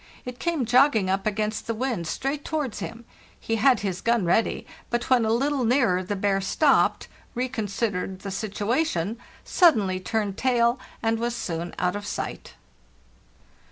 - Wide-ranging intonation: No, average, 4.2 semitones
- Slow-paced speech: No, average, 160 wpm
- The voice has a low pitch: No, high, 225 Hz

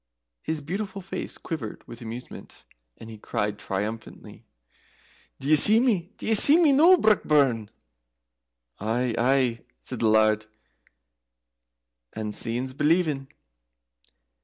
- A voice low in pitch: Yes, low, 130 Hz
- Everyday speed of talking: No, slow, 110 wpm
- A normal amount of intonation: No, wide, 8.3 semitones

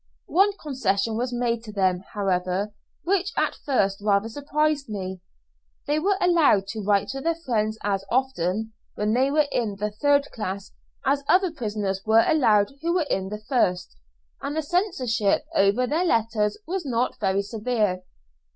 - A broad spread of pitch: Yes, wide, 6.2 semitones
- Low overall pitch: No, high, 225 Hz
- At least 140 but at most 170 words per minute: Yes, average, 160 wpm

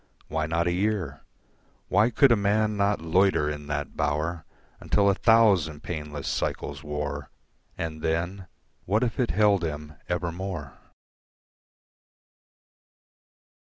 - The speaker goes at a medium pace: No, slow, 120 wpm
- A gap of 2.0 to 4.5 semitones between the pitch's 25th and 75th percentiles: No, average, 4.9 semitones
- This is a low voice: Yes, very low, 85 Hz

